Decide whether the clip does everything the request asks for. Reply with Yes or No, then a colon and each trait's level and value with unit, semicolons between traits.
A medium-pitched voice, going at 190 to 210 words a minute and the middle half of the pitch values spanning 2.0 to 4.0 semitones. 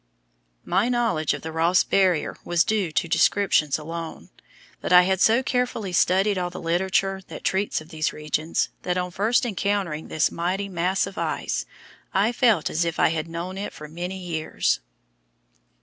No: medium, 180 Hz; average, 170 wpm; average, 3.1 semitones